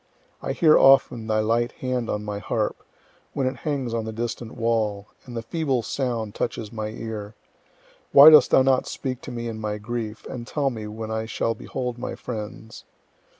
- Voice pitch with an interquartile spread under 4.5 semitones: Yes, average, 2.7 semitones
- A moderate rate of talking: Yes, average, 190 wpm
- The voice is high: No, low, 115 Hz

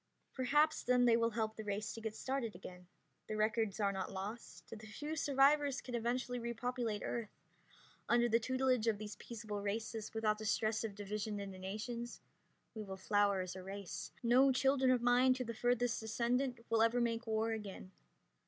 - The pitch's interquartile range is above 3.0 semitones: No, average, 2.7 semitones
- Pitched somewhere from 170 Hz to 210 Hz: No, high, 225 Hz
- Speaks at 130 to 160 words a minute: No, average, 180 wpm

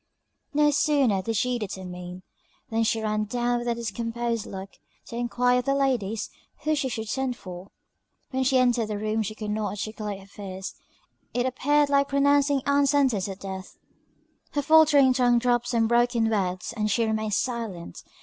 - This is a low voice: No, high, 235 Hz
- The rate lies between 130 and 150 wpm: No, average, 175 wpm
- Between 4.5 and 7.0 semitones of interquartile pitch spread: No, average, 3.8 semitones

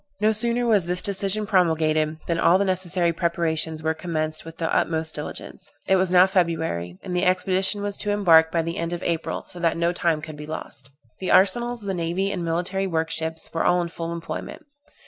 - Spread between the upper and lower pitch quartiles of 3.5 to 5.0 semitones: No, average, 2.7 semitones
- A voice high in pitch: No, medium, 170 Hz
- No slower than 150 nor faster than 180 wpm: No, fast, 205 wpm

